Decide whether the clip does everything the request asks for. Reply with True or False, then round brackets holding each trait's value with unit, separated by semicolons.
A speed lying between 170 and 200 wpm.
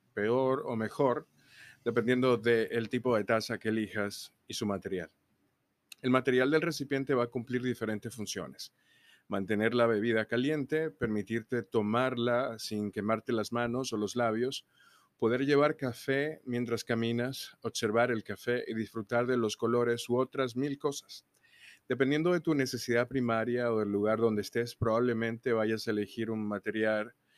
False (150 wpm)